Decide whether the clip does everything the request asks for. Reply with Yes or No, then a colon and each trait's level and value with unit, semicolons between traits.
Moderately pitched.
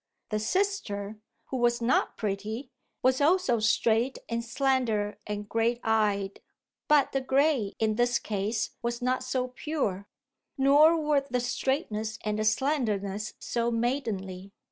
No: high, 235 Hz